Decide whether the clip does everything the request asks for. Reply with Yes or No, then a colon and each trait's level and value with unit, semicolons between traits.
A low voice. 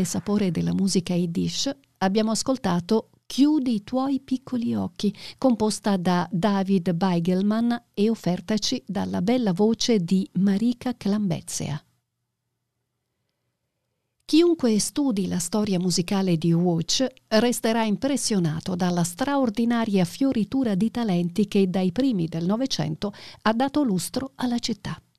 No: high, 205 Hz